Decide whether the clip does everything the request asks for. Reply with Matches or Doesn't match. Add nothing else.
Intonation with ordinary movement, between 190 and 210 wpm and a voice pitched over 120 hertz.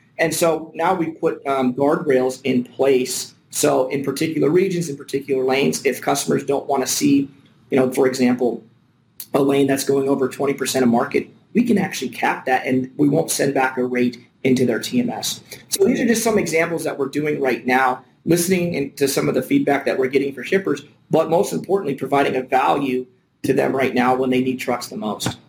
Matches